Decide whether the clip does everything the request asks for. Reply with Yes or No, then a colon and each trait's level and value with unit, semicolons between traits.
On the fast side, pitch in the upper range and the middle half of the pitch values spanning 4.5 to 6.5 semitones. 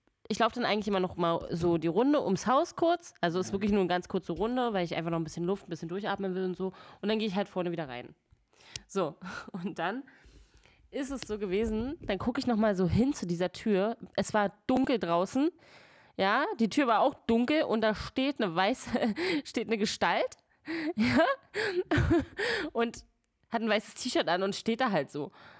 Yes: fast, 210 wpm; high, 215 Hz; wide, 5.4 semitones